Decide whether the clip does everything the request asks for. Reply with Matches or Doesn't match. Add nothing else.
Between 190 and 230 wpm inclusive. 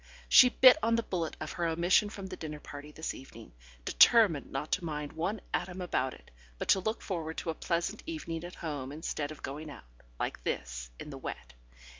Matches